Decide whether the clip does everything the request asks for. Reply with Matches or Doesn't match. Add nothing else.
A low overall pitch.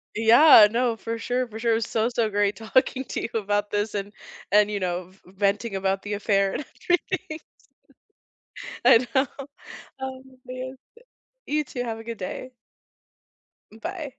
Doesn't match